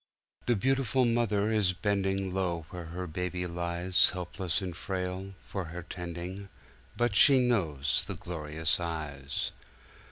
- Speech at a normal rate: No, slow, 125 wpm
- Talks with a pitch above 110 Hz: No, very low, 90 Hz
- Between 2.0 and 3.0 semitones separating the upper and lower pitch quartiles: Yes, average, 2.7 semitones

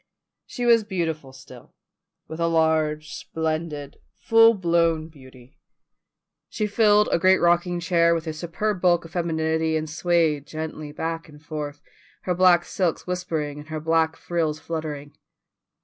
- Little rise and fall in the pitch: Yes, narrow, 2.1 semitones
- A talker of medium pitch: Yes, medium, 165 Hz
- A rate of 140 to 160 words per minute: Yes, average, 145 wpm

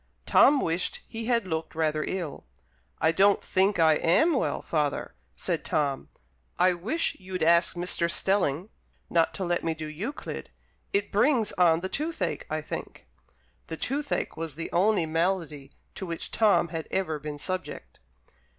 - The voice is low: No, medium, 175 Hz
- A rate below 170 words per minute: Yes, average, 155 wpm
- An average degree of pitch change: Yes, average, 3.8 semitones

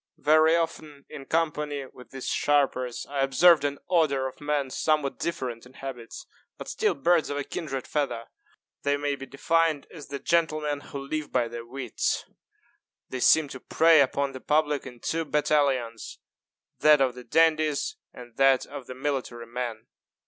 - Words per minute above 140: Yes, average, 165 wpm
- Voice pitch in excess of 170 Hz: No, medium, 140 Hz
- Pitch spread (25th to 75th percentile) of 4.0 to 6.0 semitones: No, average, 3.0 semitones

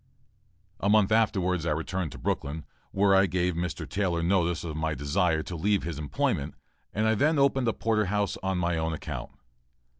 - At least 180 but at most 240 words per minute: Yes, average, 185 wpm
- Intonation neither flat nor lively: Yes, average, 4.0 semitones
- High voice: No, very low, 90 Hz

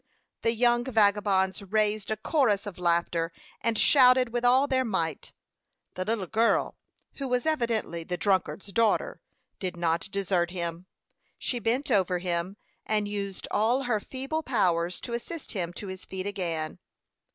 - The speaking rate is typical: Yes, average, 150 wpm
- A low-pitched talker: No, high, 205 Hz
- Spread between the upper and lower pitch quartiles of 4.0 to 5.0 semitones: Yes, average, 4.7 semitones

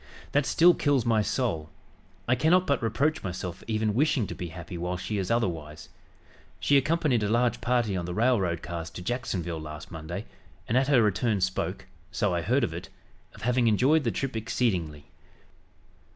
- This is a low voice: Yes, low, 110 Hz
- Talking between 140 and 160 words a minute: No, average, 180 wpm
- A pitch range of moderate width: No, wide, 6.2 semitones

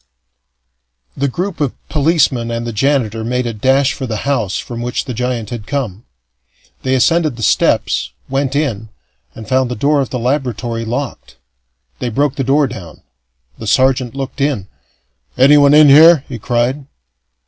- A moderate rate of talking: Yes, average, 160 wpm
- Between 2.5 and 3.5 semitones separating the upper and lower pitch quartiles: Yes, average, 3.2 semitones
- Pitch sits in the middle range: No, low, 130 Hz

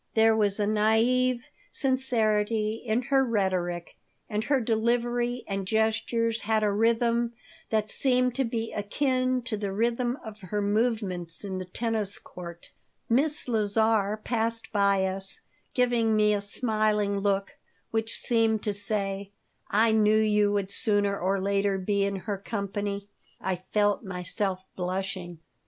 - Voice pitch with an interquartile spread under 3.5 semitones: Yes, narrow, 2.5 semitones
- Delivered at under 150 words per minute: Yes, average, 140 wpm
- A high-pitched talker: Yes, high, 215 Hz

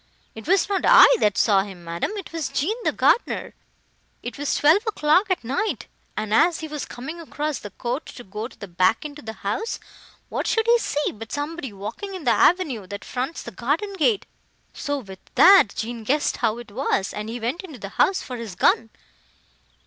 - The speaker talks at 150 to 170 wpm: No, average, 200 wpm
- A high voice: Yes, very high, 265 Hz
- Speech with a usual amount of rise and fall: No, wide, 7.4 semitones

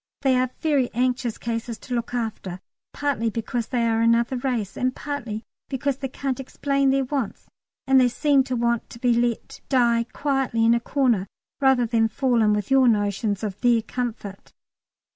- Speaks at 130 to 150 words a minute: No, average, 180 wpm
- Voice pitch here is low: No, high, 240 Hz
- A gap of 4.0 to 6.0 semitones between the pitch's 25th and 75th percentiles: No, average, 2.7 semitones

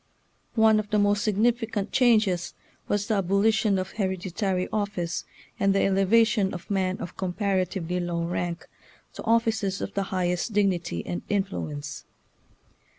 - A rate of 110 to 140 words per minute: Yes, slow, 135 wpm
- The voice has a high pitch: Yes, high, 195 Hz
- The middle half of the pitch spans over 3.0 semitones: No, average, 2.7 semitones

